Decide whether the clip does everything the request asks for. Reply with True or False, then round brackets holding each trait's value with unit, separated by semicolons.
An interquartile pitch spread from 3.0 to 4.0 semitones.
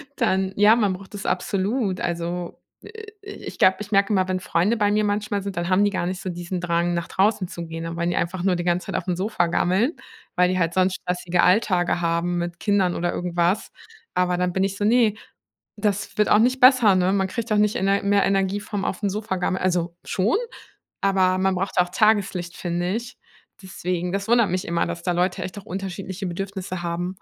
False (2.4 semitones)